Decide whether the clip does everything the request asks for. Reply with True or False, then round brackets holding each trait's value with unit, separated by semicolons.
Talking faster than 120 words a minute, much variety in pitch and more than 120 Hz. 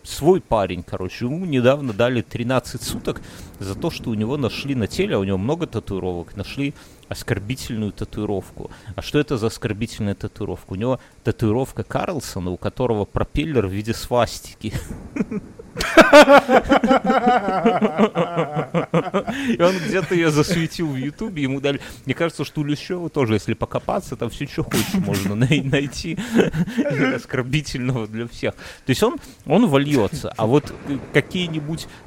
True (140 wpm; 7.0 semitones; 140 Hz)